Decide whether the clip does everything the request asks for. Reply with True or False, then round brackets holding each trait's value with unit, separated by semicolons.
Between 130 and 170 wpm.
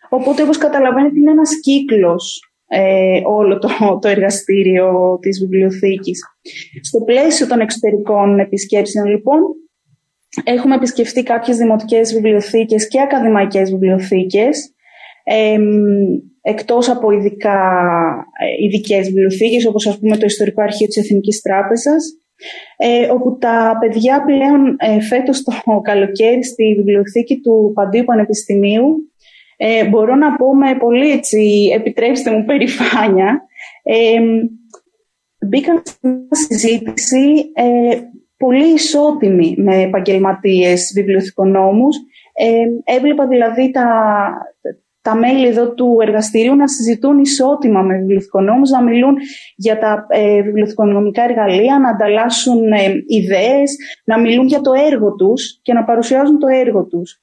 False (120 wpm)